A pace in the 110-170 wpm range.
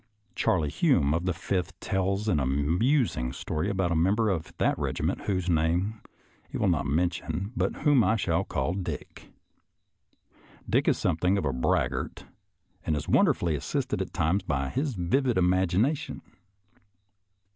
Yes: average, 150 wpm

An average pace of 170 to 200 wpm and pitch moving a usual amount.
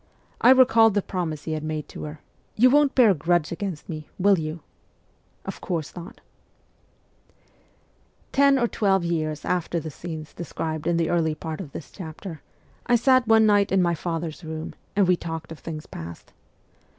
Yes: average, 185 wpm; average, 4.4 semitones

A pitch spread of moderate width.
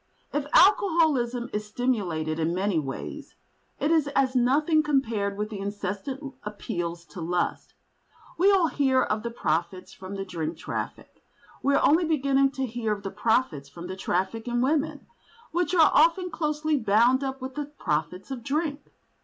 No: wide, 7.1 semitones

